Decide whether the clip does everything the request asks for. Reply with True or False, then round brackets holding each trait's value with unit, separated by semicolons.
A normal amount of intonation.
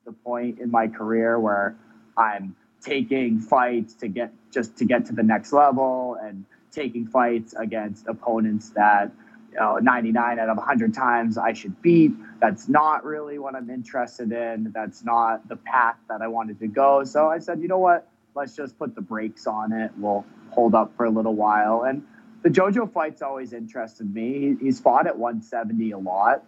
True (3.5 semitones)